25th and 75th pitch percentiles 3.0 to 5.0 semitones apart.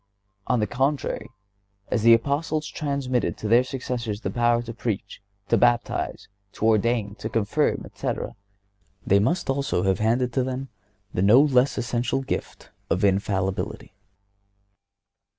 Yes: average, 3.5 semitones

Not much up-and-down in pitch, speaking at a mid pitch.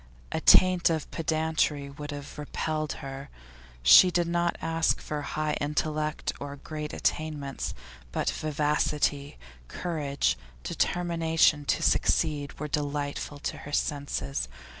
Yes: narrow, 1.9 semitones; medium, 150 Hz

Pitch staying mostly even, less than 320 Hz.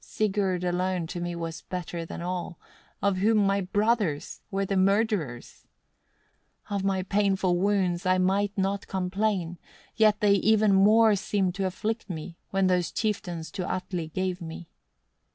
Yes: narrow, 2.3 semitones; high, 190 Hz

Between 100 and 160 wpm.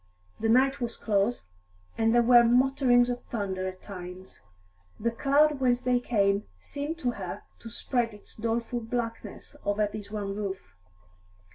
Yes: average, 150 wpm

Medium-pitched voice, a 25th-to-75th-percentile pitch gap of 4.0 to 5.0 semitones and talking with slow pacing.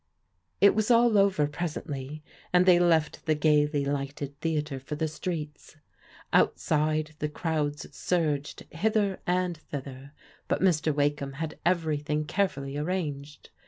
No: medium, 155 Hz; average, 3.1 semitones; slow, 125 wpm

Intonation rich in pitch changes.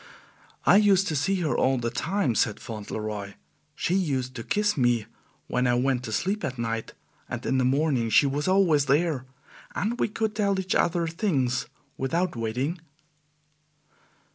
Yes: wide, 7.2 semitones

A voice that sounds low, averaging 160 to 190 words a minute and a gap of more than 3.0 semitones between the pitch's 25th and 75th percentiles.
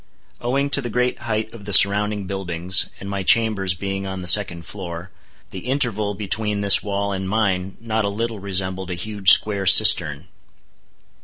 No: low, 100 Hz; average, 170 wpm; narrow, 2.4 semitones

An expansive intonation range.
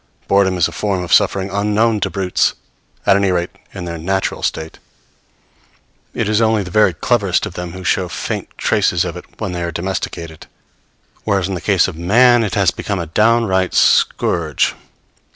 No: average, 3.0 semitones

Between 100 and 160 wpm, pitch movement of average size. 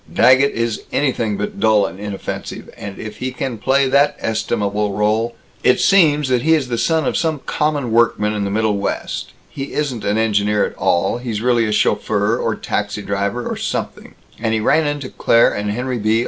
No: average, 195 wpm; average, 4.0 semitones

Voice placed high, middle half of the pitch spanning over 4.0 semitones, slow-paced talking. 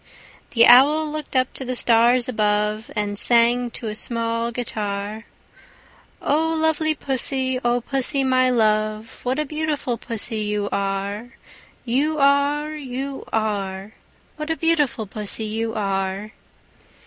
Yes: high, 240 Hz; average, 4.4 semitones; slow, 130 wpm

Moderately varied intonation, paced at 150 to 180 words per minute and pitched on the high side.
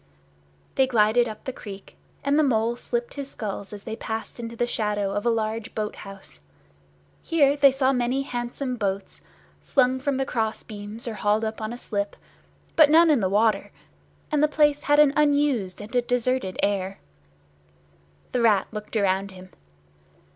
Yes: average, 4.3 semitones; average, 175 wpm; high, 230 Hz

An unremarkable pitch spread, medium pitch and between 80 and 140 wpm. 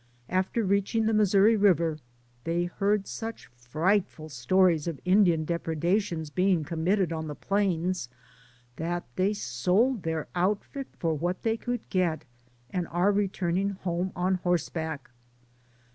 Yes: average, 3.5 semitones; medium, 180 Hz; slow, 135 wpm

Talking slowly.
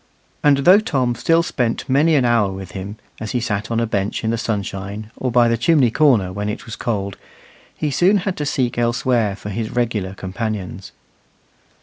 No: average, 195 wpm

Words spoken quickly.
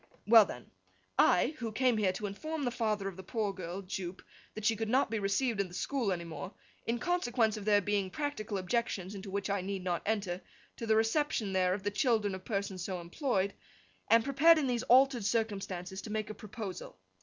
Yes: fast, 210 wpm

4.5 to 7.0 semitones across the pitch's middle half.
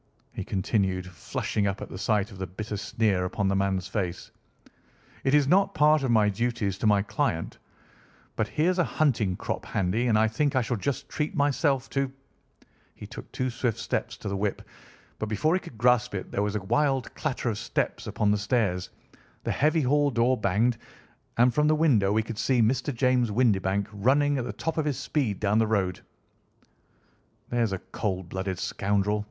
Yes: average, 5.0 semitones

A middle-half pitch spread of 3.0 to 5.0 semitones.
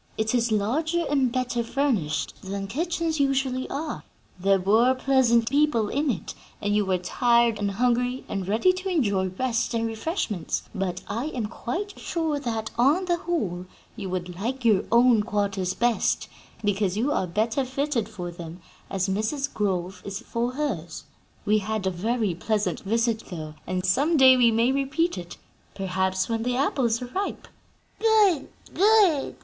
No: wide, 5.6 semitones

